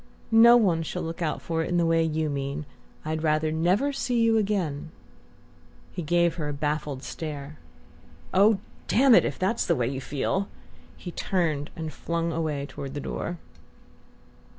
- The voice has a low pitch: No, medium, 160 Hz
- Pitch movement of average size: Yes, average, 3.4 semitones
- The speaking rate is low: No, average, 175 wpm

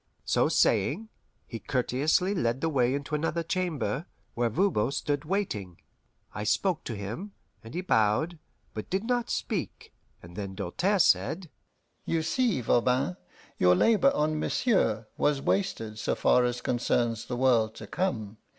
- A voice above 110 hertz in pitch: Yes, low, 135 Hz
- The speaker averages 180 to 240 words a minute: No, average, 150 wpm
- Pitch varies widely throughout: Yes, wide, 8.1 semitones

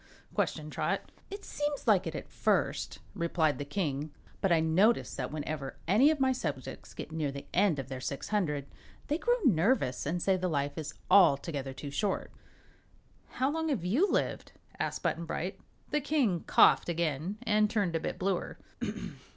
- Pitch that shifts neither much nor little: No, wide, 6.5 semitones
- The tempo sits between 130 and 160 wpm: No, average, 175 wpm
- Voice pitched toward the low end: No, medium, 175 Hz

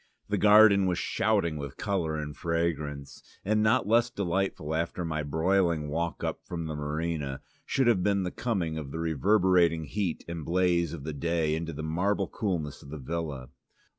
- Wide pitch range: No, average, 3.8 semitones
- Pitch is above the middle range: No, very low, 85 Hz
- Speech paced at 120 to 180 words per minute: Yes, average, 175 wpm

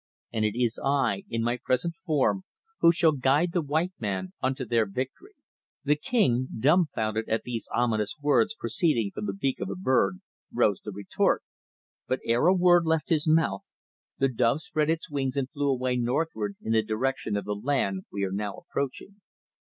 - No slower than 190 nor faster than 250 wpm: No, average, 180 wpm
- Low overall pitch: Yes, low, 130 Hz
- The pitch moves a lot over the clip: Yes, wide, 6.0 semitones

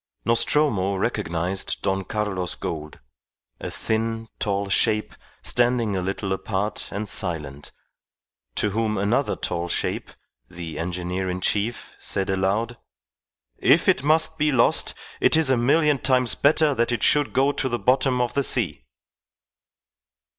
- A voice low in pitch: Yes, low, 105 Hz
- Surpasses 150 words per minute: No, average, 140 wpm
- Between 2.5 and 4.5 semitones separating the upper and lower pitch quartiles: No, average, 5.0 semitones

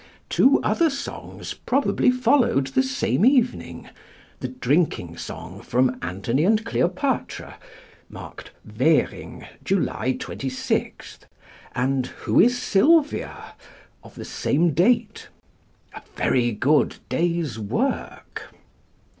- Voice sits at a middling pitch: Yes, medium, 175 Hz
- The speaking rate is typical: No, slow, 100 wpm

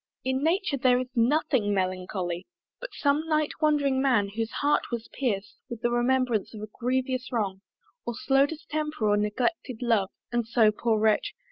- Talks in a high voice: Yes, high, 245 Hz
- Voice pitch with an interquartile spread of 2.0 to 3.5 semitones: No, average, 4.8 semitones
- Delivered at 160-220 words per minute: Yes, average, 165 wpm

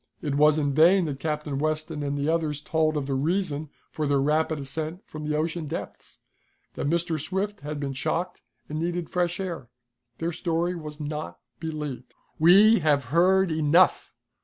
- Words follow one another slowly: No, average, 170 wpm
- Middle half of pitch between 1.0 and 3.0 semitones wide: Yes, narrow, 2.6 semitones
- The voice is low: No, medium, 155 Hz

